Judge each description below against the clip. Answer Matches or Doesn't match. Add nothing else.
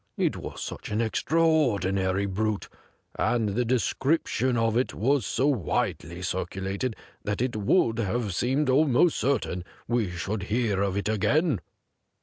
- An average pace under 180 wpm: Matches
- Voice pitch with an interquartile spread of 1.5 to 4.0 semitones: Doesn't match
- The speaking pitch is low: Matches